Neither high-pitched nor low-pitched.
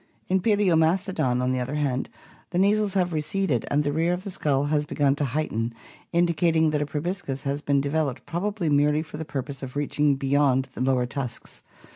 Yes: medium, 150 Hz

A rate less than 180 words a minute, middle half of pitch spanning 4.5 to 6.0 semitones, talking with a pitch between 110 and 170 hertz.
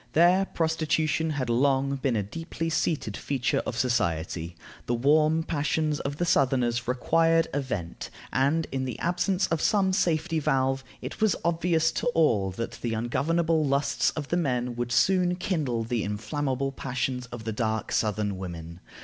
Yes: average, 160 wpm; average, 5.3 semitones; medium, 140 Hz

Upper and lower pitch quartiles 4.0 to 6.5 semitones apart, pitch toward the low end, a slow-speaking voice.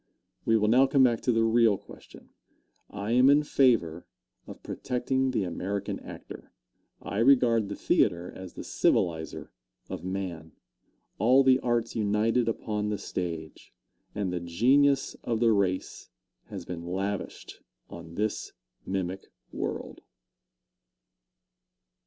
Yes: average, 4.8 semitones; low, 105 Hz; slow, 130 wpm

